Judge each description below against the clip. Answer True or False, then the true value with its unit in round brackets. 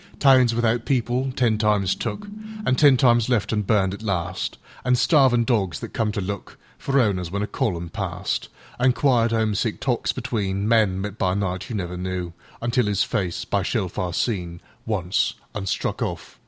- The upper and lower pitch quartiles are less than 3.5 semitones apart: False (4.3 semitones)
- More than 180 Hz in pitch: False (110 Hz)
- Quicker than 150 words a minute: False (140 wpm)